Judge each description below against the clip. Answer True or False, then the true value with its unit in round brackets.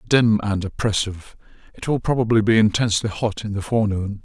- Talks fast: False (170 wpm)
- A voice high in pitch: False (105 Hz)